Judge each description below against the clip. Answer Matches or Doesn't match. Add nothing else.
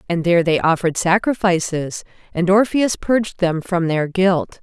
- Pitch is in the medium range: Matches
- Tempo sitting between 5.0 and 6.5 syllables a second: Doesn't match